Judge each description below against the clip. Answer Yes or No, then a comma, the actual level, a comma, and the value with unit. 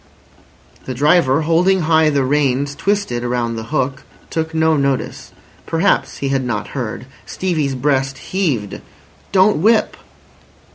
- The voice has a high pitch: No, medium, 145 Hz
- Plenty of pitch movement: No, average, 3.9 semitones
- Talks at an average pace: No, slow, 130 wpm